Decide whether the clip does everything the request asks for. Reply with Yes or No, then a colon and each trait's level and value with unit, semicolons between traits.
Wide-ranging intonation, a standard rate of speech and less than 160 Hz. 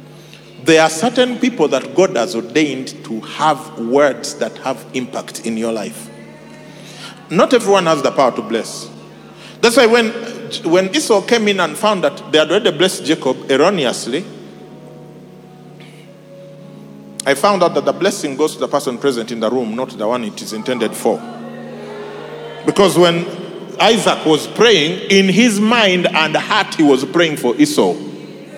No: wide, 5.9 semitones; average, 160 wpm; medium, 170 Hz